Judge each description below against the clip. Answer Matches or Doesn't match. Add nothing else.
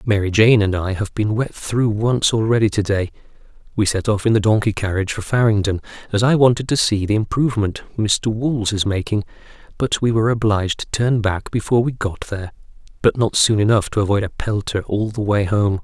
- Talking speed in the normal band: Doesn't match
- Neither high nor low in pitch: Doesn't match